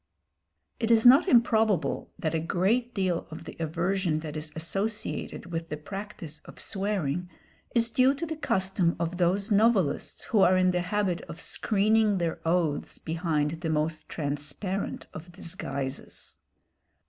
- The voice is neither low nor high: Yes, medium, 180 Hz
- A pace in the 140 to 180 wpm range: Yes, average, 150 wpm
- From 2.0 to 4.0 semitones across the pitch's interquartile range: No, average, 4.6 semitones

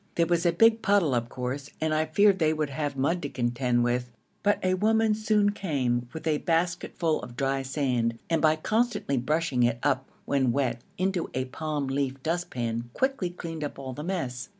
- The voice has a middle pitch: Yes, medium, 150 Hz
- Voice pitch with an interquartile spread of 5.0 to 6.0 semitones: Yes, average, 5.3 semitones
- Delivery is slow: No, average, 195 wpm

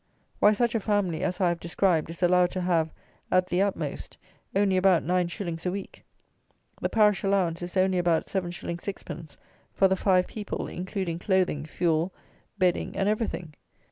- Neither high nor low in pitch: Yes, medium, 180 Hz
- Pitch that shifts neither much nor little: No, narrow, 2.3 semitones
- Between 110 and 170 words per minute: Yes, average, 165 wpm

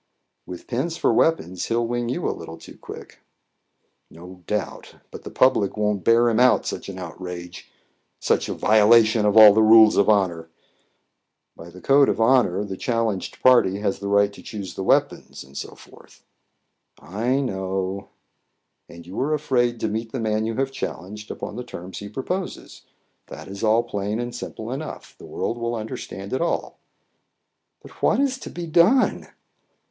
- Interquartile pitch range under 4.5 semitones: Yes, average, 4.0 semitones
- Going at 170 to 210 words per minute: Yes, average, 175 wpm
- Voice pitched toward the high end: No, low, 110 Hz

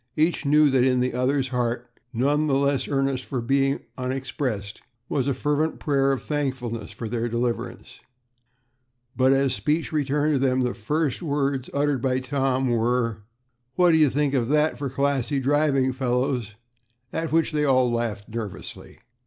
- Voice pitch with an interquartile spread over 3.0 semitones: No, average, 2.7 semitones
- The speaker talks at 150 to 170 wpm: Yes, average, 160 wpm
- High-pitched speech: No, low, 135 Hz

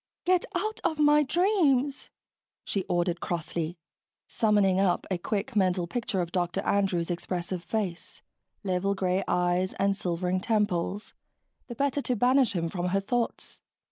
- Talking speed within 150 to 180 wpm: No, average, 140 wpm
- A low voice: No, high, 195 Hz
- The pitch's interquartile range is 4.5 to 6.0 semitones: Yes, wide, 5.4 semitones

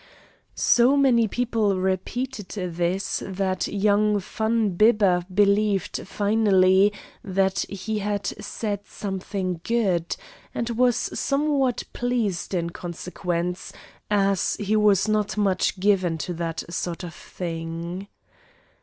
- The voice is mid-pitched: No, high, 200 Hz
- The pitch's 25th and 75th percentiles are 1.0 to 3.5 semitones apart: Yes, average, 2.9 semitones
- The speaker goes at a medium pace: No, slow, 110 wpm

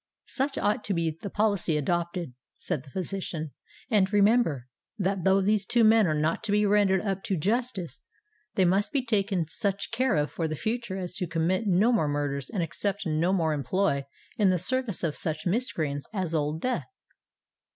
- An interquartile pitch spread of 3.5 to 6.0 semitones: Yes, average, 4.5 semitones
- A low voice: No, high, 190 Hz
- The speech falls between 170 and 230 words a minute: Yes, average, 185 wpm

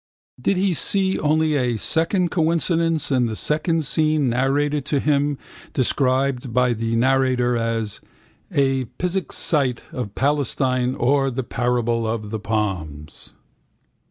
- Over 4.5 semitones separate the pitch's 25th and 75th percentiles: No, average, 4.2 semitones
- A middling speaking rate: No, slow, 130 wpm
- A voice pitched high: No, low, 135 Hz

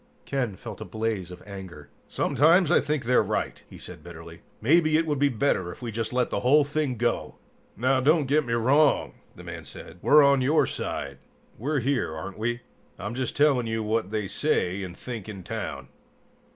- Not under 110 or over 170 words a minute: No, average, 195 wpm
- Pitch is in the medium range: No, low, 125 Hz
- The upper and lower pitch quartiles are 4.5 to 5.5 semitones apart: Yes, average, 5.0 semitones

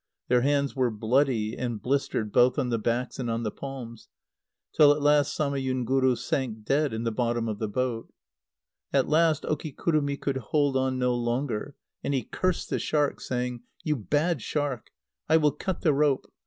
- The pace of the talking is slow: No, average, 175 wpm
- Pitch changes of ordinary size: Yes, average, 3.5 semitones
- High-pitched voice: No, low, 130 Hz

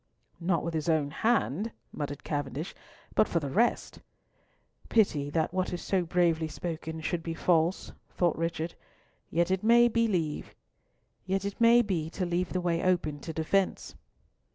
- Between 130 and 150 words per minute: Yes, average, 140 wpm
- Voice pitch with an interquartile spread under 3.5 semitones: Yes, average, 3.1 semitones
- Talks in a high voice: No, medium, 170 Hz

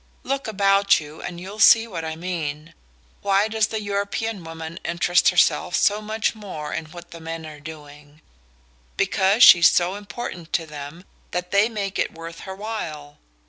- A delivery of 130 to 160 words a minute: No, average, 170 wpm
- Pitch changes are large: No, average, 4.1 semitones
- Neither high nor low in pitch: Yes, medium, 180 Hz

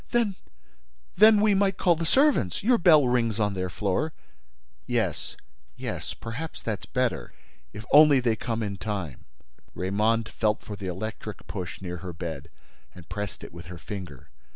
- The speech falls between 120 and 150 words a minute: Yes, average, 140 wpm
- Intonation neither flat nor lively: No, wide, 8.7 semitones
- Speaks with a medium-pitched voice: No, low, 105 Hz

